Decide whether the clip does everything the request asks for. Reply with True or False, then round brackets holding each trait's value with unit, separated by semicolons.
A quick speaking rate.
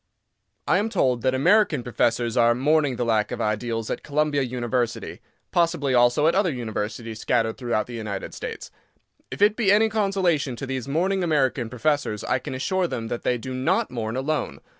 False (180 wpm)